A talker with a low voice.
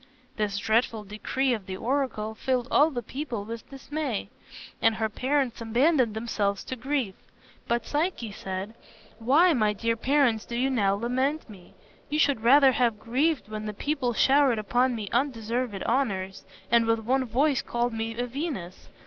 No: high, 235 Hz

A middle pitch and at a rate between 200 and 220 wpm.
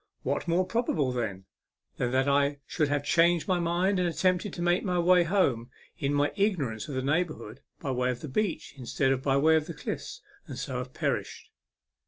Yes: medium, 145 Hz; fast, 205 wpm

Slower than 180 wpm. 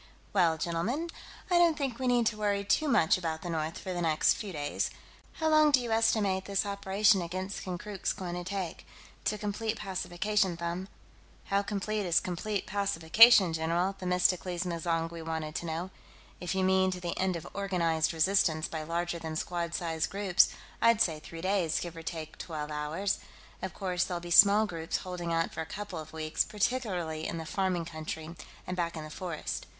No: average, 185 wpm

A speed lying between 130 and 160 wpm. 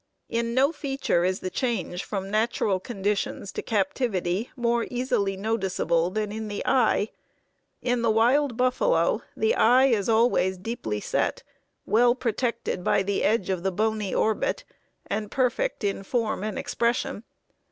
Yes: average, 145 wpm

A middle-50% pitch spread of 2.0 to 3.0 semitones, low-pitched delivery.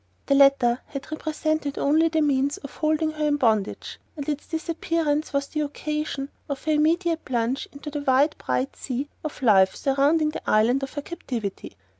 No: narrow, 2.4 semitones; very high, 290 Hz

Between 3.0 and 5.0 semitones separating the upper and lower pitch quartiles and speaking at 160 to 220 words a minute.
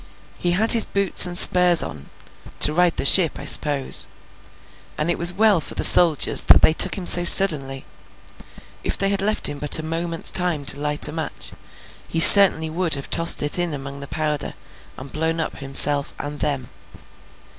Yes: average, 3.5 semitones; average, 185 wpm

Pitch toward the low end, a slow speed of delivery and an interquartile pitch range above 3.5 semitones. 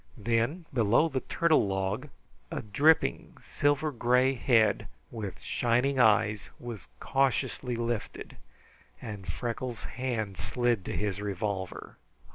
Yes: low, 115 Hz; slow, 110 wpm; average, 3.9 semitones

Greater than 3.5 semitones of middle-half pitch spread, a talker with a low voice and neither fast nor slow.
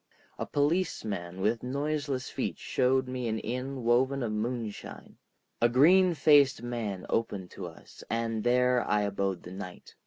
Yes: average, 4.1 semitones; low, 120 Hz; average, 150 wpm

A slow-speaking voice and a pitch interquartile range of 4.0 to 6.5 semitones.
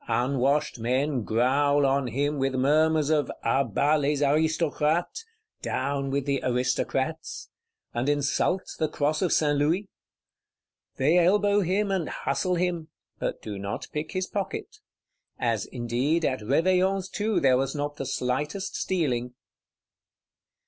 Yes: slow, 130 wpm; average, 4.5 semitones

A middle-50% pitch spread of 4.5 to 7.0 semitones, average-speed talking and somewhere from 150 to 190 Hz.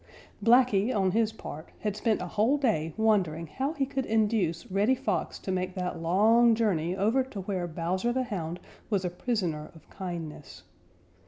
No: average, 4.8 semitones; average, 170 wpm; high, 200 Hz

